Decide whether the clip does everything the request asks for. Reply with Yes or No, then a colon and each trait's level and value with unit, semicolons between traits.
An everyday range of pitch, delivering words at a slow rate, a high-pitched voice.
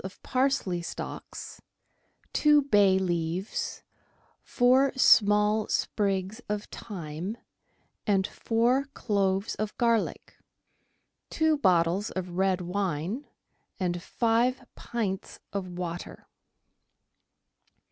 Yes: average, 4.2 semitones; slow, 85 wpm; high, 200 Hz